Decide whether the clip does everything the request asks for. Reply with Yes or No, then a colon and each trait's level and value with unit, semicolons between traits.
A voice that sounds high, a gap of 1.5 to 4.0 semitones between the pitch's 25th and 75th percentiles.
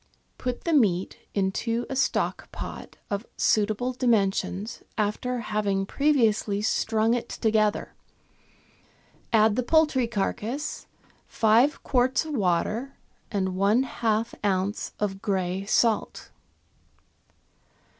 Yes: high, 220 Hz; average, 3.6 semitones